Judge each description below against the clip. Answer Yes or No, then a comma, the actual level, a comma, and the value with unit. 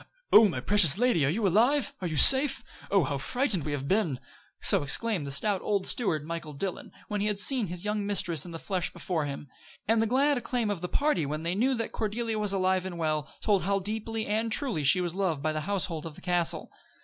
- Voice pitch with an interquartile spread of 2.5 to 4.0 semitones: No, average, 5.2 semitones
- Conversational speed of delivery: No, fast, 235 wpm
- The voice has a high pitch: Yes, high, 195 Hz